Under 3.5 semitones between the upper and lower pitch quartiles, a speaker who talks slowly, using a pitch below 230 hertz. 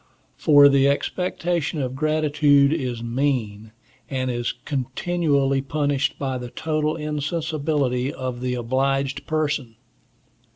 Yes: average, 2.9 semitones; slow, 110 wpm; medium, 140 Hz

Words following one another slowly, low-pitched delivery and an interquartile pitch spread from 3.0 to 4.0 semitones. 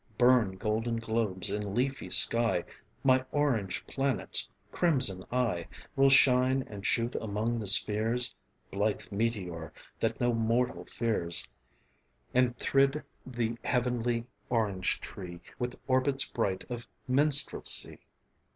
Yes: slow, 115 wpm; low, 115 Hz; average, 3.5 semitones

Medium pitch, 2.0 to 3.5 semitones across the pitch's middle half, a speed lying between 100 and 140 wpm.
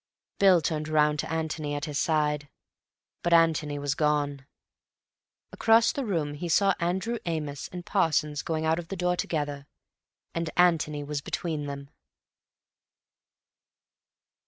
Yes: medium, 155 Hz; average, 2.7 semitones; slow, 135 wpm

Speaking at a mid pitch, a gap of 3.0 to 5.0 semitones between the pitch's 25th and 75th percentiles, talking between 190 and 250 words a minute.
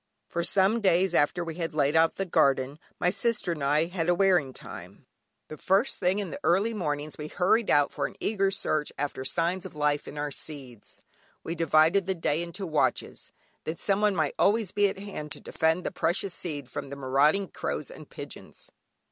Yes: medium, 165 Hz; average, 4.5 semitones; average, 200 wpm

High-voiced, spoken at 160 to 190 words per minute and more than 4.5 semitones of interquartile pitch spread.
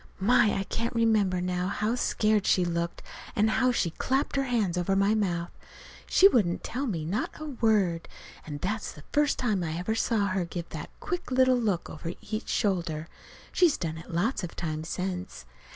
Yes: high, 195 Hz; average, 185 wpm; average, 5.0 semitones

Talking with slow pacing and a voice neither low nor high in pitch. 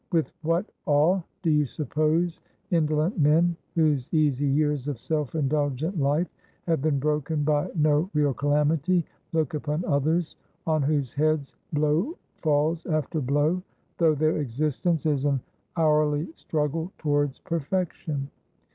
Yes: slow, 130 wpm; medium, 150 Hz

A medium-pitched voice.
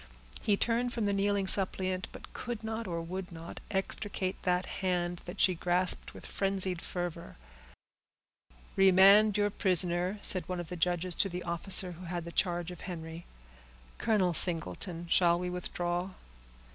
Yes: medium, 180 Hz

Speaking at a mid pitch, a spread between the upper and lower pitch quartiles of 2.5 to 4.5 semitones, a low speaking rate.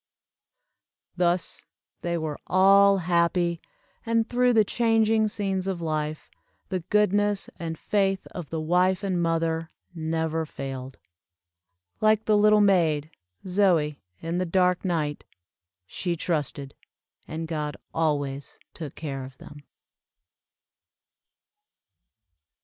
Yes: medium, 170 Hz; average, 3.9 semitones; slow, 110 wpm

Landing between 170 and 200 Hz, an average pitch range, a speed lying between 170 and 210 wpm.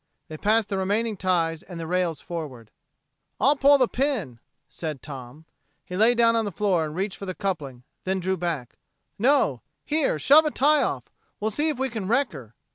No: high, 190 Hz; wide, 6.8 semitones; average, 200 wpm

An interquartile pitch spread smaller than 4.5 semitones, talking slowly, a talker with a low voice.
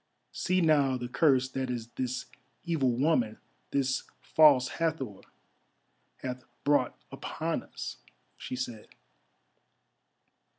Yes: average, 3.2 semitones; slow, 95 wpm; low, 130 Hz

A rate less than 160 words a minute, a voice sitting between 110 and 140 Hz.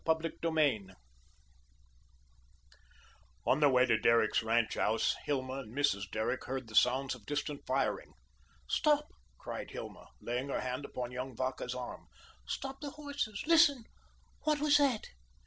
Yes: average, 140 wpm; low, 135 Hz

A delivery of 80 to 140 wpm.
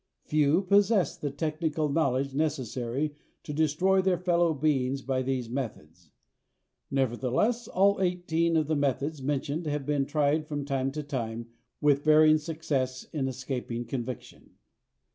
Yes: slow, 135 wpm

